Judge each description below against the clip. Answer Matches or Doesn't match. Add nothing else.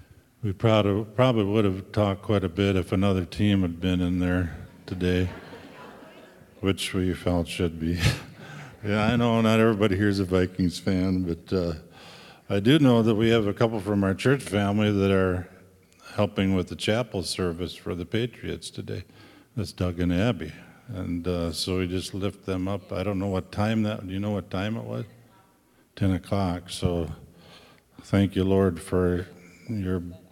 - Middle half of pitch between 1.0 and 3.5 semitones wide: Matches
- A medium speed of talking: Matches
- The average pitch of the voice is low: Matches